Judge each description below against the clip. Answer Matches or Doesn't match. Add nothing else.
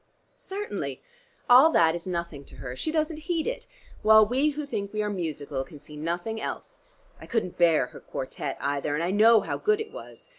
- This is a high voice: Matches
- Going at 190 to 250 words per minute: Matches